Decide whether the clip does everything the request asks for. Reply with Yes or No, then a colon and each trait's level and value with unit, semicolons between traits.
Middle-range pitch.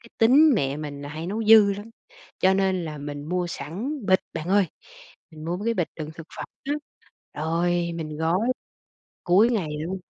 Yes: medium, 175 Hz